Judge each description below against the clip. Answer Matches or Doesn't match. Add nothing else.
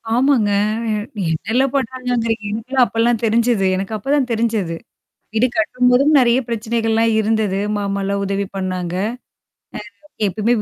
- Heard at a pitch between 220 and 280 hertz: Matches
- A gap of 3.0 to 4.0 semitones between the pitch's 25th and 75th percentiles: Matches